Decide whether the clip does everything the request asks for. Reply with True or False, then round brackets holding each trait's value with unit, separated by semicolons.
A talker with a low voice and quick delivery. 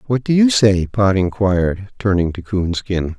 False (100 Hz; 170 wpm)